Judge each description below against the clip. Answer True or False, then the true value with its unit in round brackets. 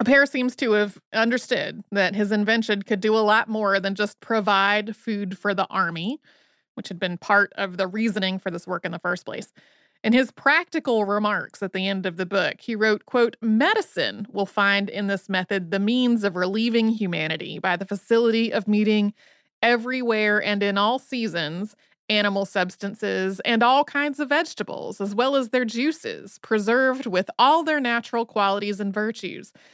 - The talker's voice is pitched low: False (210 Hz)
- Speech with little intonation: False (3.0 semitones)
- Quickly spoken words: False (180 wpm)